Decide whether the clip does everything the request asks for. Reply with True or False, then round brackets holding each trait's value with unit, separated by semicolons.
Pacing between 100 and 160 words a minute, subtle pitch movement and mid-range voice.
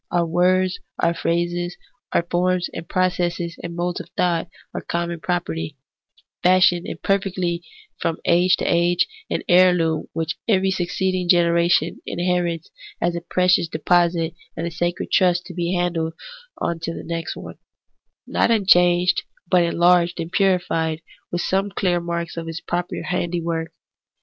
True (155 wpm; 1.1 semitones; 175 Hz)